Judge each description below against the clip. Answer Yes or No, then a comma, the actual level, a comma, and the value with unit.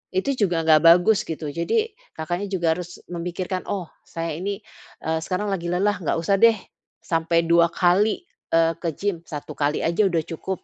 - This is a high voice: No, medium, 175 Hz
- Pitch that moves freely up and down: No, average, 2.9 semitones